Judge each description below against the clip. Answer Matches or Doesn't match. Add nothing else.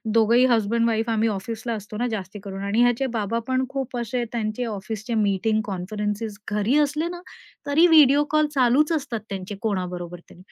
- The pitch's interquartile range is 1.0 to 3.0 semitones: Doesn't match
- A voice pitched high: Matches